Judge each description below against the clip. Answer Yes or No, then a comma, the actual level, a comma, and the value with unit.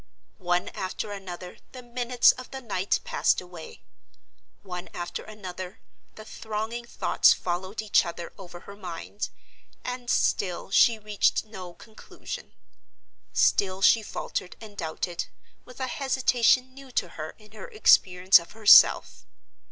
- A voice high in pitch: Yes, high, 205 Hz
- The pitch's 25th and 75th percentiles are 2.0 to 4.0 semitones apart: No, average, 4.8 semitones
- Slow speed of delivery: Yes, slow, 130 wpm